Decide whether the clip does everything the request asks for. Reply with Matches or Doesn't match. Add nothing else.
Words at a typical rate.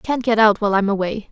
Doesn't match